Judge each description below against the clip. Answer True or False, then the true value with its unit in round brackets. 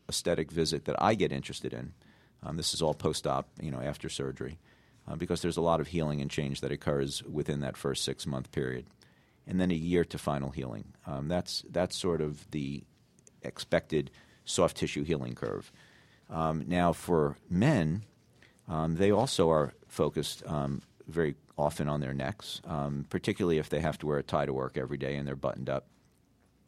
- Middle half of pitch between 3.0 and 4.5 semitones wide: True (3.5 semitones)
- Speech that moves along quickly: False (185 wpm)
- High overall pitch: False (75 Hz)